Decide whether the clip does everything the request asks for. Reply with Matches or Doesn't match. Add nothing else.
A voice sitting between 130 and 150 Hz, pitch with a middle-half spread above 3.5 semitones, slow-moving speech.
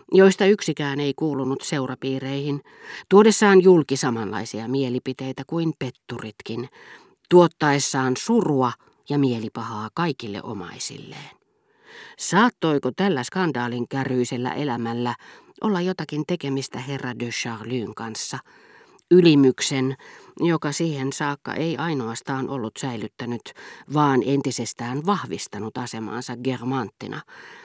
Matches